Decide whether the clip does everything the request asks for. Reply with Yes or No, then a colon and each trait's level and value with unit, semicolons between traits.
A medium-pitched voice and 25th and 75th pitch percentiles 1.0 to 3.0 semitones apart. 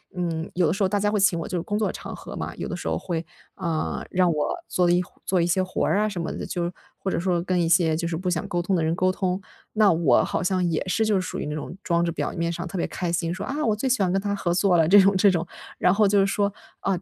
Yes: medium, 180 Hz; narrow, 2.5 semitones